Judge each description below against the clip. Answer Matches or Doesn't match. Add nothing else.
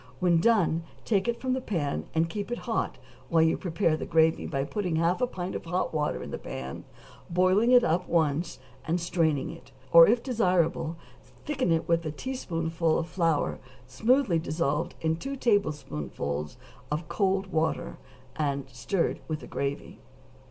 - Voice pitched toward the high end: Doesn't match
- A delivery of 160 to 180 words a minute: Matches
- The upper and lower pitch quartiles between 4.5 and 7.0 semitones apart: Doesn't match